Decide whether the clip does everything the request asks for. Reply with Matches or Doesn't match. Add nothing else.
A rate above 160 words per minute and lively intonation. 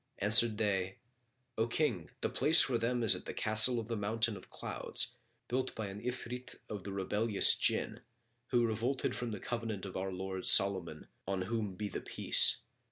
Doesn't match